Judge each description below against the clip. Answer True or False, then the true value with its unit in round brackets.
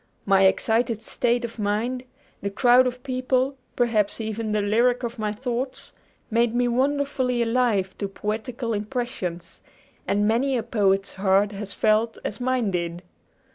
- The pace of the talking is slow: False (145 wpm)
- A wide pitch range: False (3.3 semitones)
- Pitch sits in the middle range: False (230 Hz)